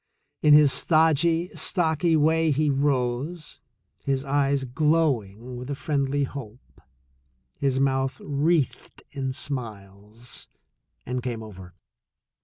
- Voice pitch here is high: No, medium, 140 Hz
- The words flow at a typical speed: No, slow, 105 wpm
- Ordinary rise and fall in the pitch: Yes, average, 3.5 semitones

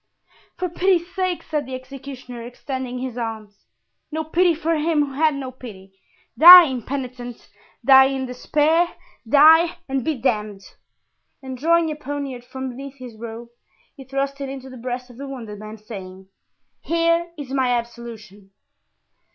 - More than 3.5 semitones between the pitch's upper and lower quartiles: Yes, average, 4.0 semitones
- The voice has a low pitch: No, very high, 265 Hz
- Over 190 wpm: No, average, 150 wpm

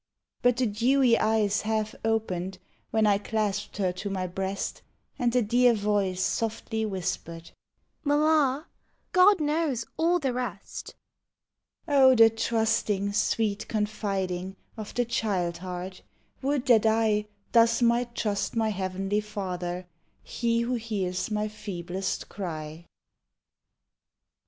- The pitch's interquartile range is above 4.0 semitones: No, average, 3.5 semitones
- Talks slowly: Yes, slow, 125 wpm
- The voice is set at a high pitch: Yes, high, 215 Hz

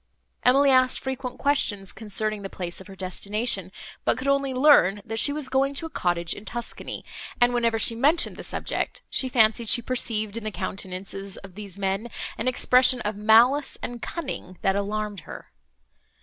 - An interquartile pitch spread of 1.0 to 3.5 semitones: No, average, 4.4 semitones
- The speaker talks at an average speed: Yes, average, 175 wpm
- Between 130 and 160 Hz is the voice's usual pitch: No, high, 225 Hz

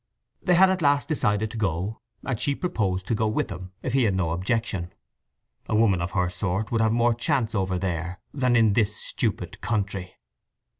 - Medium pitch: No, low, 105 Hz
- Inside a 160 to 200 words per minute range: Yes, average, 195 wpm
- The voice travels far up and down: No, average, 4.1 semitones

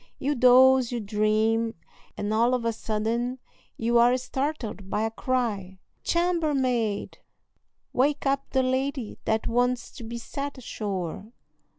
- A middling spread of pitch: Yes, average, 3.1 semitones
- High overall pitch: Yes, high, 240 Hz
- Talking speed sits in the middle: No, slow, 130 wpm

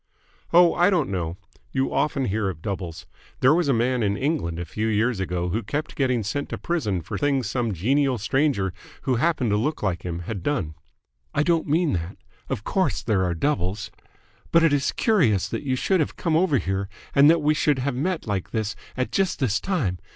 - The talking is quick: Yes, fast, 210 wpm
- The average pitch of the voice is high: No, low, 125 Hz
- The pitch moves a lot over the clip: Yes, wide, 7.3 semitones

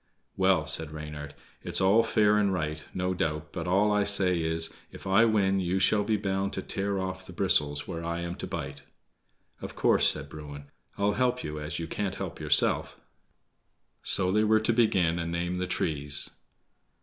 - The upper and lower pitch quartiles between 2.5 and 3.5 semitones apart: No, average, 4.2 semitones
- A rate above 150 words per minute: Yes, average, 185 wpm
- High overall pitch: No, very low, 90 Hz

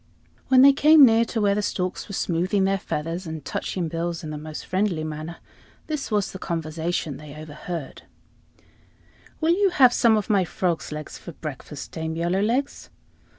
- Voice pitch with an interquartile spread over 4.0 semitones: Yes, average, 5.1 semitones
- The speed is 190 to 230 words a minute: No, average, 170 wpm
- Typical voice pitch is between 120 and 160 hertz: No, medium, 180 Hz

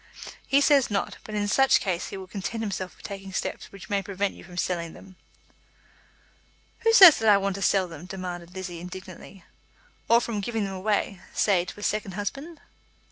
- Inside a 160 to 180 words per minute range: No, average, 190 wpm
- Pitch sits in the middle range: No, high, 195 Hz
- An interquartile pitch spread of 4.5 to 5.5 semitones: No, narrow, 2.6 semitones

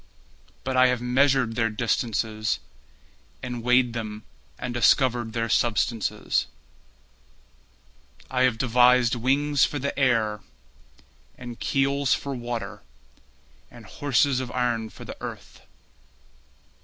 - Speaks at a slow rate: Yes, slow, 110 wpm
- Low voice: Yes, low, 125 Hz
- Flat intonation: Yes, narrow, 2.2 semitones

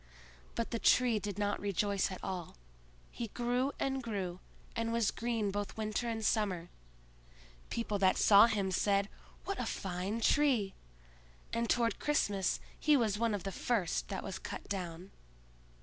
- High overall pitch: Yes, high, 210 Hz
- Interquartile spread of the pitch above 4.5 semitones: No, average, 3.2 semitones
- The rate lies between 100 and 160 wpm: Yes, average, 155 wpm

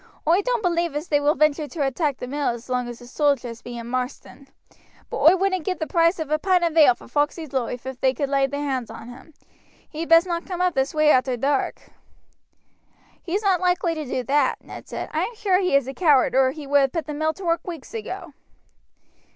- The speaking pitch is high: Yes, very high, 295 Hz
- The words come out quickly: Yes, fast, 235 wpm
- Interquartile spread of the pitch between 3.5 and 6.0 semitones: Yes, average, 4.4 semitones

